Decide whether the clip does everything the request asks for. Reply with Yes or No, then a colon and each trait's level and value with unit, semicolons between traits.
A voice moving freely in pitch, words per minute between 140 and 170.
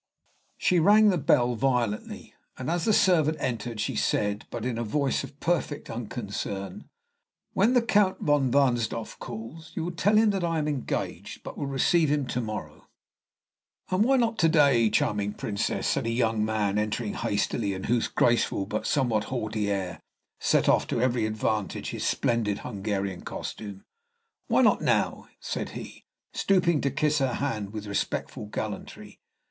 Yes: wide, 6.5 semitones; average, 165 wpm